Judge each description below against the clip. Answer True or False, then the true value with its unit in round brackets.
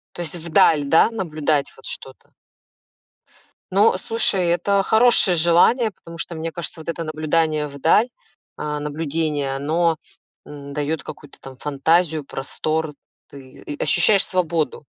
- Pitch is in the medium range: True (160 Hz)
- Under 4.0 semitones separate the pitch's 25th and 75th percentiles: True (2.8 semitones)